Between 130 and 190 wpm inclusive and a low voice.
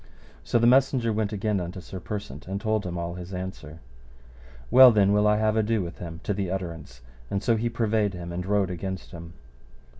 No: fast, 205 wpm; low, 100 Hz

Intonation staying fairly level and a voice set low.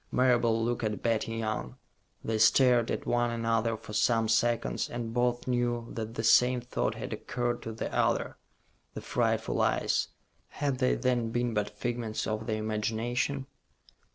Yes: narrow, 1.5 semitones; low, 115 Hz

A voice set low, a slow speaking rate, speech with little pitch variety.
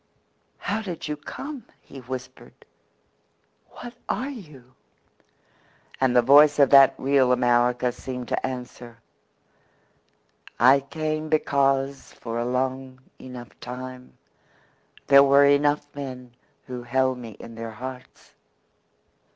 Yes: low, 130 Hz; slow, 115 wpm; narrow, 2.3 semitones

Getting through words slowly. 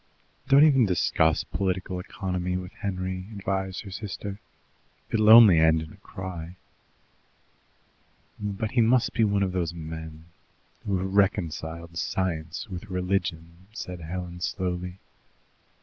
Yes: slow, 125 wpm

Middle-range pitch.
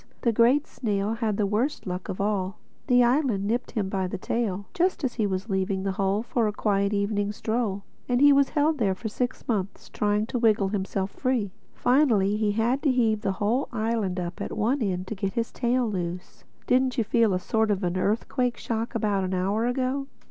No: high, 215 Hz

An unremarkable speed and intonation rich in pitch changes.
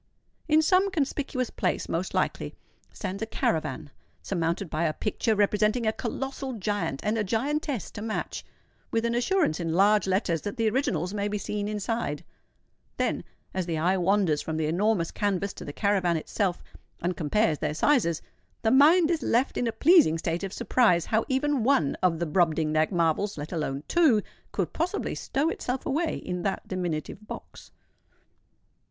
Yes: average, 160 wpm; wide, 6.4 semitones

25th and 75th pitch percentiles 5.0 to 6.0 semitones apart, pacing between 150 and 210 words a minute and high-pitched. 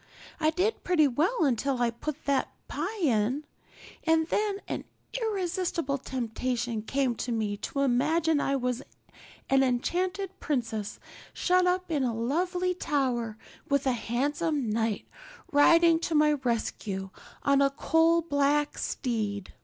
No: wide, 5.6 semitones; slow, 135 wpm; very high, 280 Hz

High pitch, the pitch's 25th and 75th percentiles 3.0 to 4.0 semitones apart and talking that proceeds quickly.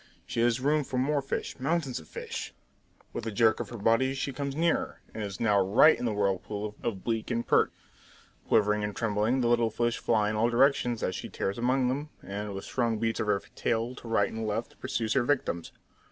No: low, 115 Hz; average, 3.5 semitones; fast, 215 wpm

